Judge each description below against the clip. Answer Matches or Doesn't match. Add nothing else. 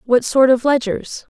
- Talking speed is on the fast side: Doesn't match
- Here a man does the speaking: Doesn't match